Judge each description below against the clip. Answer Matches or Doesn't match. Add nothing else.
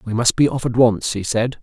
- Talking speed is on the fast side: Matches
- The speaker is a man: Matches